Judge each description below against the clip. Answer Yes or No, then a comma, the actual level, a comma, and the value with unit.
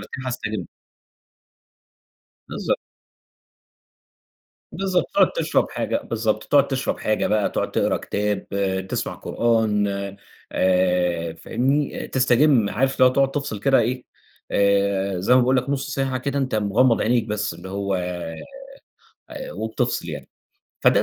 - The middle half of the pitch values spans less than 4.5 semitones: No, average, 5.0 semitones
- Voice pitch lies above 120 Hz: No, low, 115 Hz